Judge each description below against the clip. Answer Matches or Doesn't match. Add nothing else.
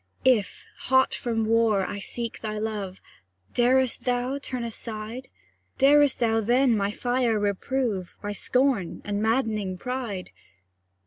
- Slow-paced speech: Matches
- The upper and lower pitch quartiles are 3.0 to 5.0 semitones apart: Matches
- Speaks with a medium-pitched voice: Doesn't match